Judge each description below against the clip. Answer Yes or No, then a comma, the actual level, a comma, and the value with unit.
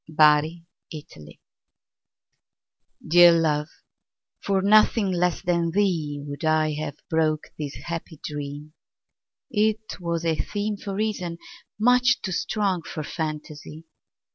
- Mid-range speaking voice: Yes, medium, 165 Hz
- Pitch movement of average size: Yes, average, 4.3 semitones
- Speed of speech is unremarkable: No, slow, 100 wpm